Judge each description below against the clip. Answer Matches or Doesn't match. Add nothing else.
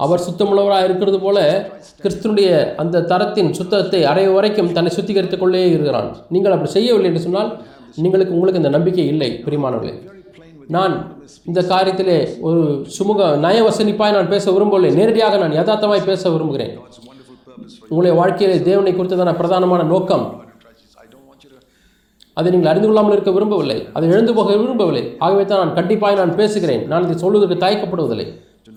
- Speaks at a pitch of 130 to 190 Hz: Matches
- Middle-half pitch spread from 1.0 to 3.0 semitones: Matches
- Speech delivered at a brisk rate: Matches